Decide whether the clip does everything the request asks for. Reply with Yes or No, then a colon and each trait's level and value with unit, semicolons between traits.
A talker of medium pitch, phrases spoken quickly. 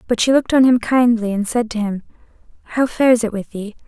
No: high, 230 Hz; fast, 230 wpm